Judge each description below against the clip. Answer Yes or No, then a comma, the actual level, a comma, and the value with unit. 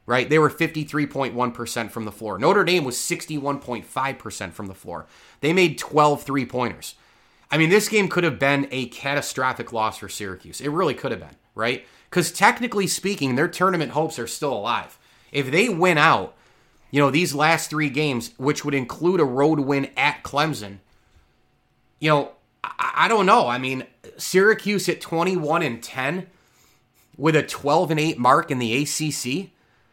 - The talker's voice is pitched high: No, medium, 140 Hz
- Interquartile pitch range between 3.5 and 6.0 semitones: Yes, average, 4.9 semitones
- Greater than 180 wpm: No, average, 170 wpm